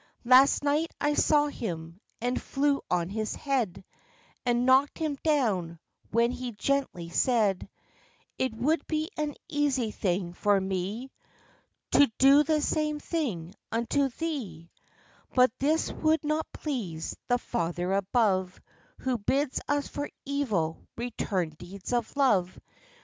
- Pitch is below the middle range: No, high, 245 Hz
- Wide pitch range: Yes, wide, 7.0 semitones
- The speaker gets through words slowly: Yes, slow, 130 wpm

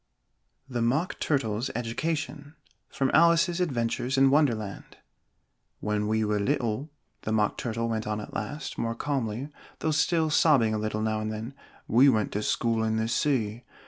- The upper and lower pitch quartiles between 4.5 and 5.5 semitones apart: Yes, average, 4.8 semitones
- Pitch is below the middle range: Yes, low, 115 Hz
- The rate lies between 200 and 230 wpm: No, average, 160 wpm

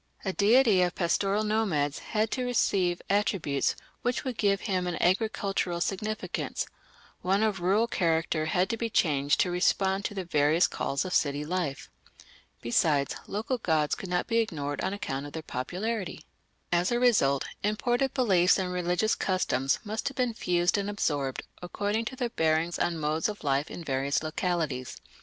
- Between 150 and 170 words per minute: Yes, average, 165 wpm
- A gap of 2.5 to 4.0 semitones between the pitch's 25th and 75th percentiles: No, average, 5.1 semitones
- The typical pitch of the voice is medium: Yes, medium, 180 Hz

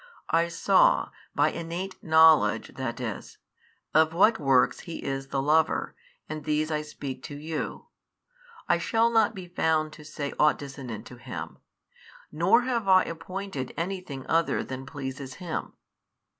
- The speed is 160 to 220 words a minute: No, average, 150 wpm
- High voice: No, medium, 160 Hz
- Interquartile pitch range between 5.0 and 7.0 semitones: No, average, 4.4 semitones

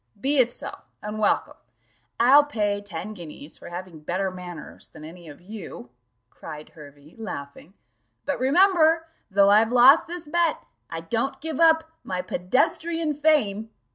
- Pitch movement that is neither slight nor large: No, wide, 8.8 semitones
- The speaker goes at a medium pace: Yes, average, 145 wpm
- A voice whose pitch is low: No, high, 215 Hz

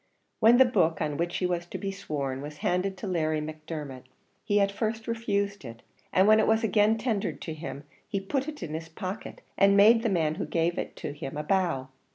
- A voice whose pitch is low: No, medium, 185 Hz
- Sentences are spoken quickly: Yes, fast, 220 wpm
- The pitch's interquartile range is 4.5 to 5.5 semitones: Yes, average, 5.2 semitones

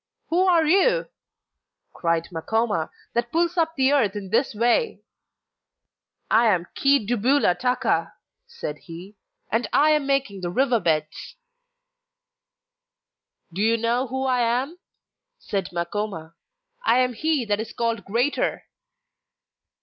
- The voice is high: Yes, high, 235 Hz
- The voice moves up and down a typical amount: No, wide, 5.7 semitones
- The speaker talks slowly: Yes, slow, 125 wpm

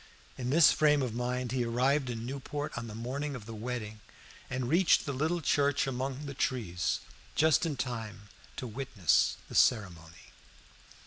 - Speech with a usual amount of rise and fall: Yes, average, 3.7 semitones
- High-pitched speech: No, low, 125 Hz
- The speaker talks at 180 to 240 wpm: No, average, 165 wpm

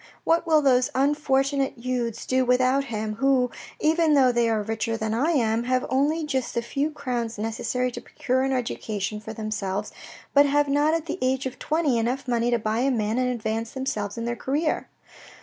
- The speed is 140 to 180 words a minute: No, average, 195 wpm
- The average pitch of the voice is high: Yes, very high, 250 Hz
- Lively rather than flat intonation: No, average, 3.5 semitones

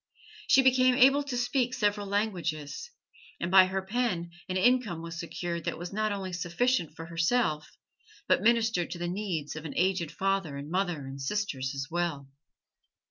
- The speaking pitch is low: No, medium, 185 Hz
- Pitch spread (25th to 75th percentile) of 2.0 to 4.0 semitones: No, average, 4.8 semitones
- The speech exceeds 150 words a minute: Yes, average, 170 wpm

